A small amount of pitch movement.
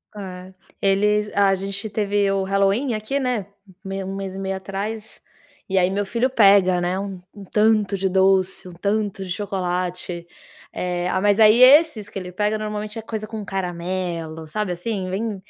Yes: narrow, 2.2 semitones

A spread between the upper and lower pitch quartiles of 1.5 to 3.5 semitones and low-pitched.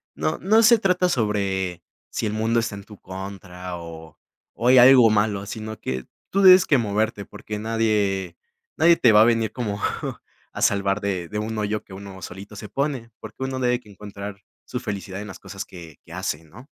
Yes: average, 3.2 semitones; low, 105 Hz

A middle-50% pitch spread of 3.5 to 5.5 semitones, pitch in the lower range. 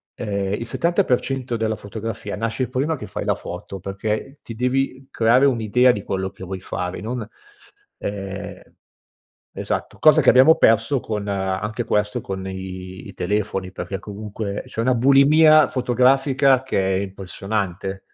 Yes: average, 4.7 semitones; low, 110 Hz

